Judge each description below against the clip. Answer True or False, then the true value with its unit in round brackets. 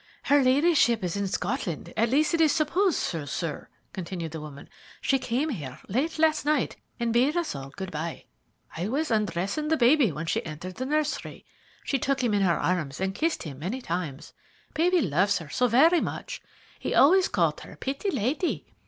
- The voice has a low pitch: False (235 Hz)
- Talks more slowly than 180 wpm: False (185 wpm)